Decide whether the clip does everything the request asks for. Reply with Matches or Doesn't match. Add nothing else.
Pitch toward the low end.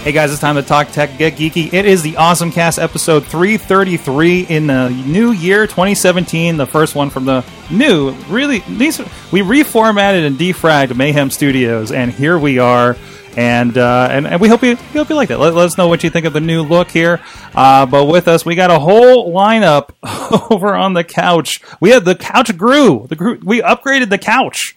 Doesn't match